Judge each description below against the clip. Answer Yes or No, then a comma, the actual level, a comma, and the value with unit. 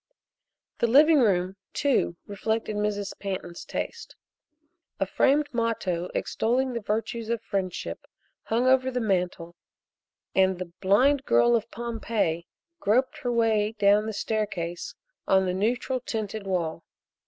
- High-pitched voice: Yes, high, 215 Hz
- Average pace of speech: No, slow, 130 wpm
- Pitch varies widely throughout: No, average, 4.0 semitones